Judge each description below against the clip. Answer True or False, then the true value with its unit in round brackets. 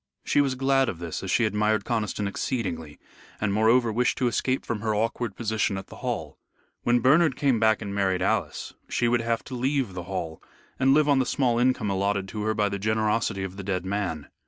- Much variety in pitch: False (3.8 semitones)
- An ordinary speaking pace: False (215 wpm)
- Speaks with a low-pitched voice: True (110 Hz)